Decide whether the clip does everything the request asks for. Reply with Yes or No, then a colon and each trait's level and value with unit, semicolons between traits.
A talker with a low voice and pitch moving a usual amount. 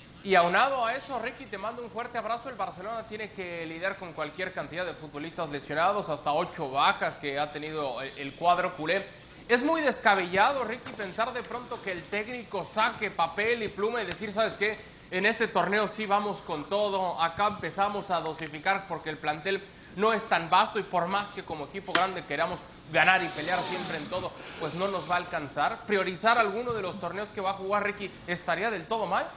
No: high, 190 Hz; average, 4.1 semitones